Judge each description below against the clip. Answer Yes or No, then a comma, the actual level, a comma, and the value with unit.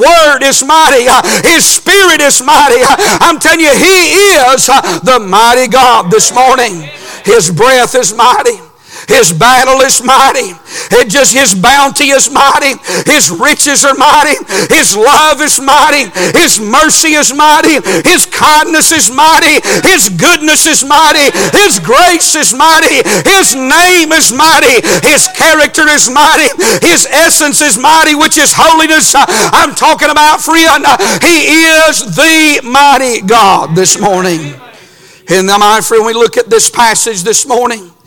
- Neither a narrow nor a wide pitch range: Yes, average, 4.2 semitones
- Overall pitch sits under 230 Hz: No, very high, 295 Hz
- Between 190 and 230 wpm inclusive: No, average, 145 wpm